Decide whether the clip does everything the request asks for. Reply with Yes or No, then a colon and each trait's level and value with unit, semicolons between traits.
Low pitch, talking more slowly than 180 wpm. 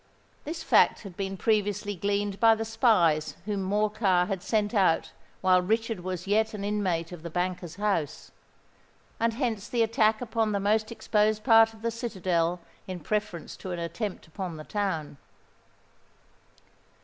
No: high, 205 Hz; average, 155 wpm